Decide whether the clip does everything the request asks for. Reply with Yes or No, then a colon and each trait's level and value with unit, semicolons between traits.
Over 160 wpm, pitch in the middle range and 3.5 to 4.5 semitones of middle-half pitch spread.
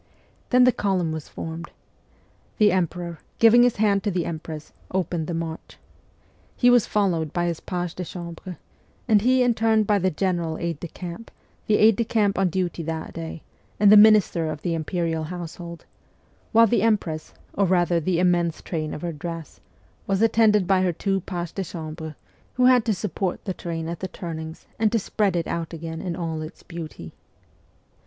Yes: average, 185 wpm; medium, 175 Hz; average, 3.8 semitones